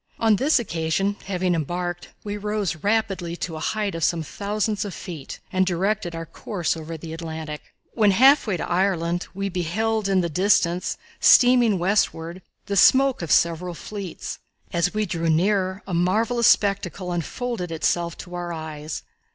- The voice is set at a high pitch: No, medium, 180 Hz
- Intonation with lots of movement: No, average, 3.5 semitones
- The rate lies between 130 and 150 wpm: No, average, 160 wpm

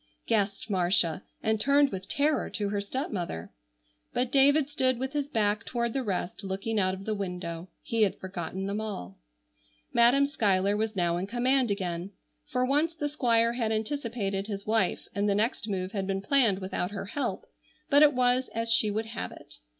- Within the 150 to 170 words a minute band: No, average, 185 wpm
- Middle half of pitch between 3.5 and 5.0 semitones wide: Yes, average, 4.5 semitones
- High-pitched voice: Yes, high, 215 Hz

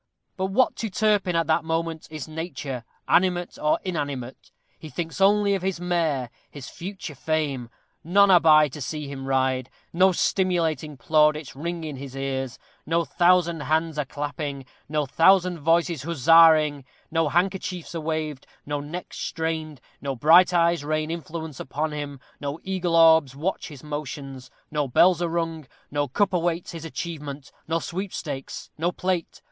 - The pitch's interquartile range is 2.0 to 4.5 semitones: Yes, average, 3.0 semitones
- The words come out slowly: No, average, 155 wpm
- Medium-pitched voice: Yes, medium, 160 Hz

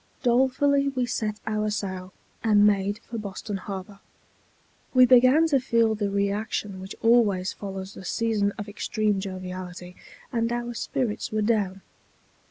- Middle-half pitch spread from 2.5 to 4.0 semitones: Yes, average, 3.2 semitones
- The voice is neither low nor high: No, high, 210 Hz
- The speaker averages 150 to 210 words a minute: No, average, 140 wpm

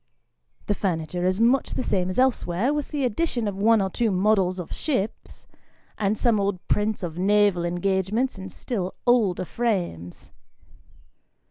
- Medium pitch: No, high, 200 Hz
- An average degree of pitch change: Yes, average, 4.1 semitones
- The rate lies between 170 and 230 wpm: No, average, 150 wpm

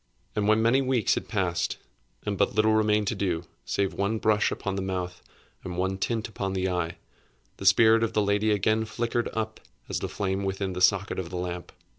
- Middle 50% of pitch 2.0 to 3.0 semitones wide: Yes, narrow, 2.6 semitones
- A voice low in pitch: Yes, low, 100 Hz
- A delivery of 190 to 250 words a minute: Yes, fast, 205 wpm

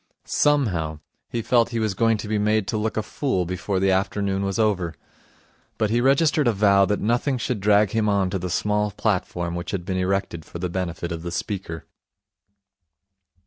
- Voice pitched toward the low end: Yes, low, 100 Hz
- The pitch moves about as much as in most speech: Yes, average, 3.0 semitones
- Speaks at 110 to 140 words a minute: No, average, 190 wpm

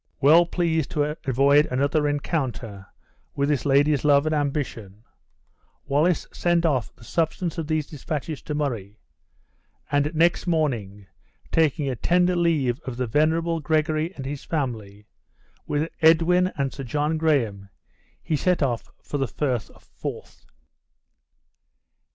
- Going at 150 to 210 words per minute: No, slow, 135 wpm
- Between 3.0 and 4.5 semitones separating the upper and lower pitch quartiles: Yes, average, 3.6 semitones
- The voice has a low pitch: No, medium, 145 Hz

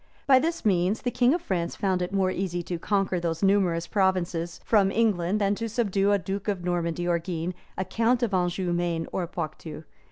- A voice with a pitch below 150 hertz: No, medium, 185 Hz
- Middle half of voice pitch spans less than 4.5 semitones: Yes, average, 2.8 semitones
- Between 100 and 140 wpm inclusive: No, average, 200 wpm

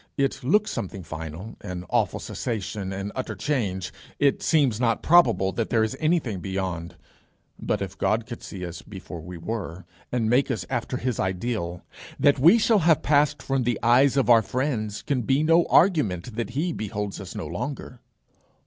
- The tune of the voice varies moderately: No, wide, 6.3 semitones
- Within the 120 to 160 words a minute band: No, average, 175 wpm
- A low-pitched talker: Yes, low, 115 Hz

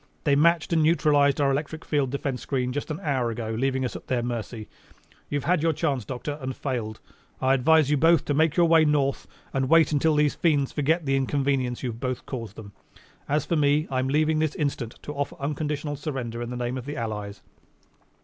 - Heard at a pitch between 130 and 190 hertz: Yes, medium, 140 Hz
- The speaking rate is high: Yes, fast, 215 wpm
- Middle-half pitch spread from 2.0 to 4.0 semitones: Yes, average, 3.2 semitones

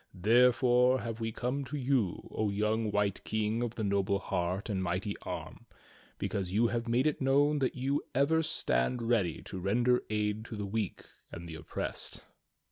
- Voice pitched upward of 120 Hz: No, low, 110 Hz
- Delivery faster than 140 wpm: Yes, average, 180 wpm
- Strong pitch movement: No, average, 4.0 semitones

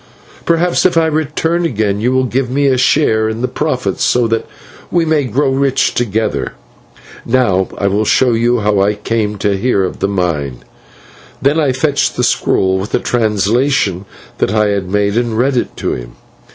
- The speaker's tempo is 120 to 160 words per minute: No, average, 190 wpm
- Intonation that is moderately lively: Yes, average, 5.0 semitones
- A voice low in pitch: Yes, low, 115 Hz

